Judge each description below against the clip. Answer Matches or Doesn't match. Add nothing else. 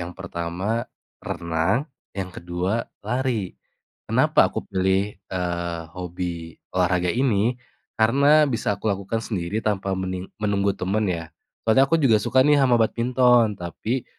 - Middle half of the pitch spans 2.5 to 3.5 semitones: Doesn't match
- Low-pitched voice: Matches